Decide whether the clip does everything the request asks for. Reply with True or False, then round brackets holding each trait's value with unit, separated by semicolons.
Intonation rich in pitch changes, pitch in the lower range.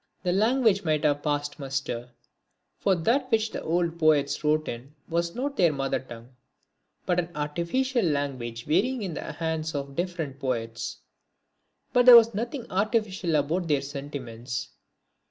False (5.9 semitones; 160 Hz)